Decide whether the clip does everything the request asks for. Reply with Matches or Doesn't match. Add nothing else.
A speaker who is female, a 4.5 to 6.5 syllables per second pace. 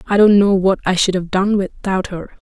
Matches